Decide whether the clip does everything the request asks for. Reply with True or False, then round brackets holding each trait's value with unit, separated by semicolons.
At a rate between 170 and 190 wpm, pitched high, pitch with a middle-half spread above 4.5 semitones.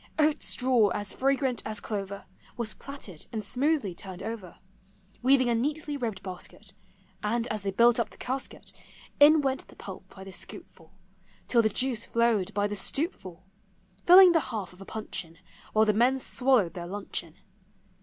True (175 wpm; 225 Hz; 5.1 semitones)